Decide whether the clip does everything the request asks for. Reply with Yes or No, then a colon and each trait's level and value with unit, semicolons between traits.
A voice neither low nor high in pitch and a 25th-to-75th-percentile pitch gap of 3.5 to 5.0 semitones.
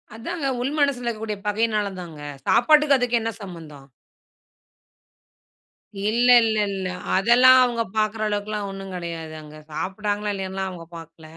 No: high, 210 Hz; average, 3.9 semitones